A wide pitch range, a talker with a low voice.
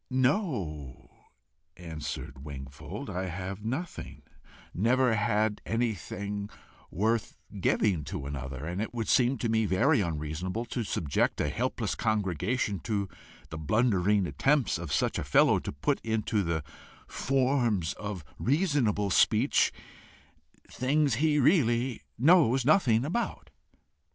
Yes: wide, 6.2 semitones; low, 110 Hz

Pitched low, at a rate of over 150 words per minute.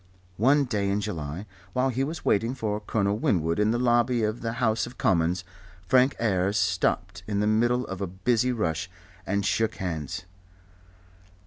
Yes: low, 105 Hz; average, 165 wpm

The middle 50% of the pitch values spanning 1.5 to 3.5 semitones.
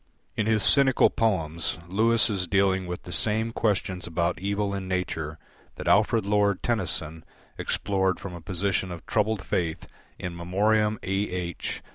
Yes: average, 3.1 semitones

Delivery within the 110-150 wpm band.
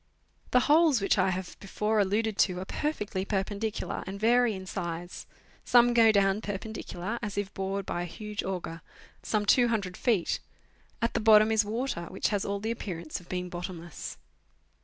No: average, 175 wpm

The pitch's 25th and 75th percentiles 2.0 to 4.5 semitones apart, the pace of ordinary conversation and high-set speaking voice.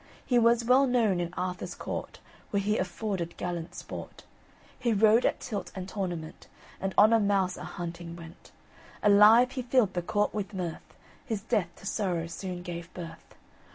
Yes: average, 4.0 semitones; average, 170 wpm; high, 195 Hz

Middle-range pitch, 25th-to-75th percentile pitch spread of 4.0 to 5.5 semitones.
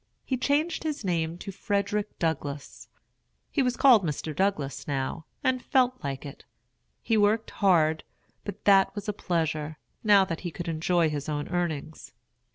Yes: medium, 175 Hz; average, 5.2 semitones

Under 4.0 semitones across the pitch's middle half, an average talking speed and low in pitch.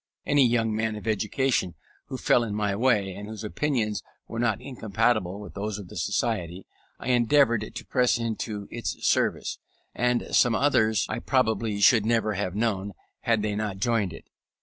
Yes: narrow, 2.6 semitones; average, 170 wpm; low, 110 Hz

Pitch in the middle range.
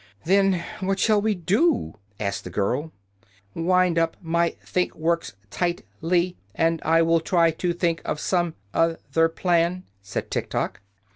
Yes: medium, 170 Hz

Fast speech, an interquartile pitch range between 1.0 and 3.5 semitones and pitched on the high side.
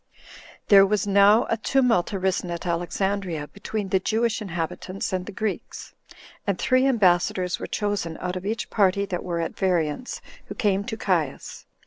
No: average, 165 wpm; average, 3.0 semitones; high, 195 Hz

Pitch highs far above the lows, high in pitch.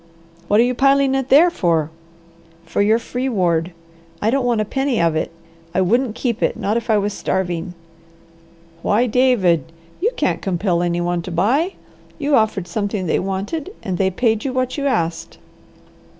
Yes: wide, 6.4 semitones; high, 210 Hz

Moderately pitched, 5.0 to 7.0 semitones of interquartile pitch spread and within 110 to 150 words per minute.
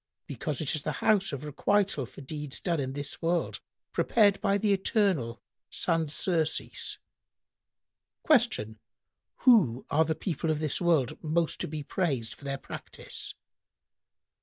Yes: medium, 155 Hz; wide, 5.4 semitones; average, 145 wpm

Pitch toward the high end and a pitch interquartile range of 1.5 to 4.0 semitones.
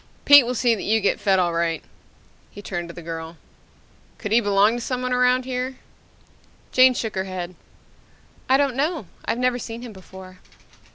No: high, 225 Hz; average, 5.2 semitones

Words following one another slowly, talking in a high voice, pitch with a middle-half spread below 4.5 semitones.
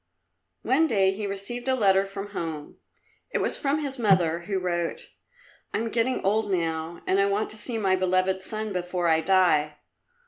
No: average, 180 wpm; high, 195 Hz; average, 3.5 semitones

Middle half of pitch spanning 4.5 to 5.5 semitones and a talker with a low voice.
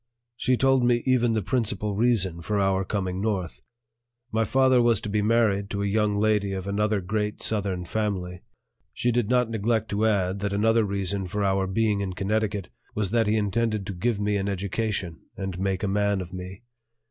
No: narrow, 2.4 semitones; low, 105 Hz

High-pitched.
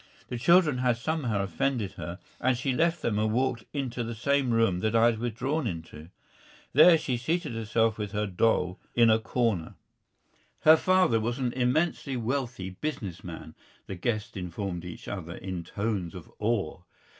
No: low, 115 Hz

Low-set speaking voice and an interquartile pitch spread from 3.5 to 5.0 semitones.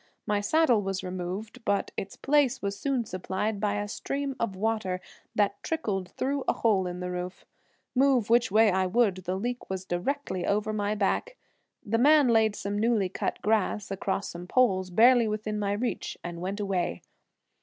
No: high, 205 Hz; average, 3.8 semitones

